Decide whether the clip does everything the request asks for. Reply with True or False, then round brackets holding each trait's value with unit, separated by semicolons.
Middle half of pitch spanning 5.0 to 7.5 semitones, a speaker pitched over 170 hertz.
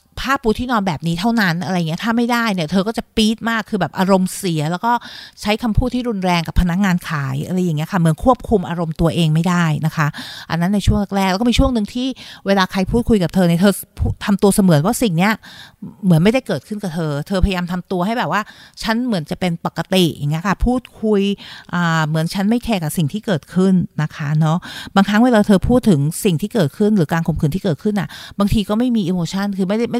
False (4.5 semitones; 190 Hz)